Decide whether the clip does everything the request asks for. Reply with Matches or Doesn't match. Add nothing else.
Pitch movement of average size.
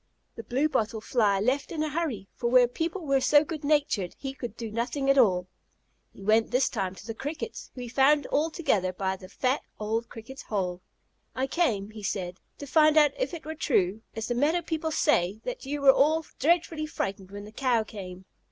Doesn't match